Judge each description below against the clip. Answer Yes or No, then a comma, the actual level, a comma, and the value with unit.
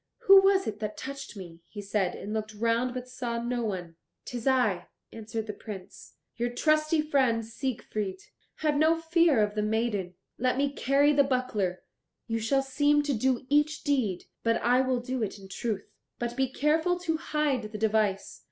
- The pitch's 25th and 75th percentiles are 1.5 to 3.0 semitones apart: No, average, 4.9 semitones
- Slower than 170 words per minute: No, average, 180 wpm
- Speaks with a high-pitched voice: Yes, high, 240 Hz